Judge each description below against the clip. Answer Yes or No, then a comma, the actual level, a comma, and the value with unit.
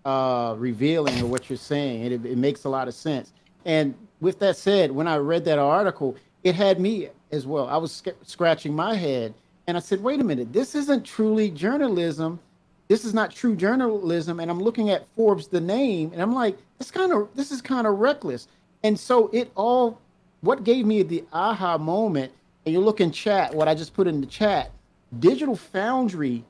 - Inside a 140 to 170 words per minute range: No, fast, 205 wpm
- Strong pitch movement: Yes, wide, 6.3 semitones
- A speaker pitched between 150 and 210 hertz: Yes, medium, 185 Hz